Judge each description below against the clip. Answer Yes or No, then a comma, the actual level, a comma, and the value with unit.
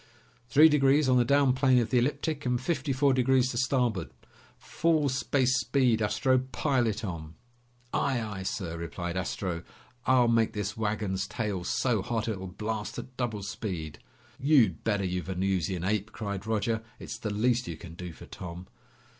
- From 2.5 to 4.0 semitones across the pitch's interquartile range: No, wide, 5.4 semitones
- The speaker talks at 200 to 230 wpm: No, average, 170 wpm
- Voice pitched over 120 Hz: No, low, 110 Hz